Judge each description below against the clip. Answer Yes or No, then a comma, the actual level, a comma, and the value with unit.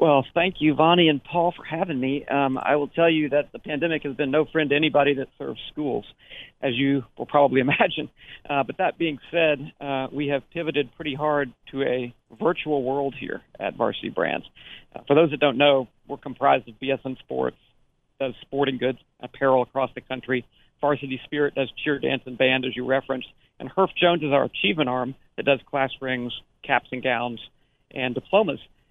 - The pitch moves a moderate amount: No, narrow, 2.3 semitones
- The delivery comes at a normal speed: Yes, average, 195 wpm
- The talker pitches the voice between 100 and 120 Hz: No, medium, 140 Hz